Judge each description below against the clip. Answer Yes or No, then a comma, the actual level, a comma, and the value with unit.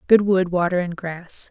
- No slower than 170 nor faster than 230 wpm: Yes, average, 200 wpm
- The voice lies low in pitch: No, medium, 180 Hz